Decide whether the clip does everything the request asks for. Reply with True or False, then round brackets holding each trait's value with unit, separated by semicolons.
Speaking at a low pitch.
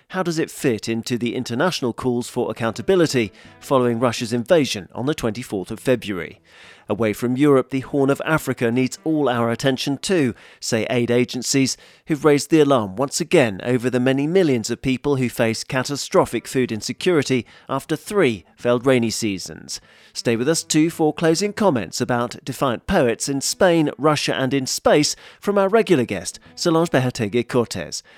True (130 Hz)